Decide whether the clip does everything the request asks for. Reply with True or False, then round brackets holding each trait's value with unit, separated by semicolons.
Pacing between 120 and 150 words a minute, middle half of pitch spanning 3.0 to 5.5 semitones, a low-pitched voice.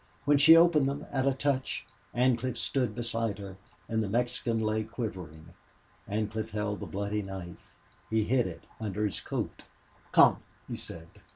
False (160 wpm; 4.0 semitones; 110 Hz)